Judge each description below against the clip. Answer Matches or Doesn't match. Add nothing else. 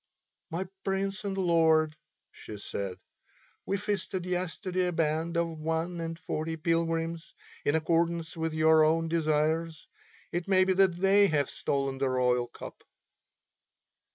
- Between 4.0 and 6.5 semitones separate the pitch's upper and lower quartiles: Doesn't match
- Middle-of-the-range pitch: Matches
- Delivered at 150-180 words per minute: Doesn't match